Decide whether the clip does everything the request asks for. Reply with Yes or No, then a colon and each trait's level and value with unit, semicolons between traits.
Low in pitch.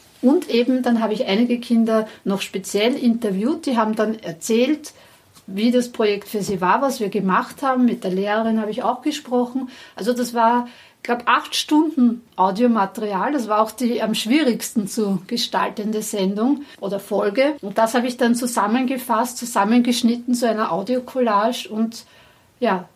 No: high, 230 Hz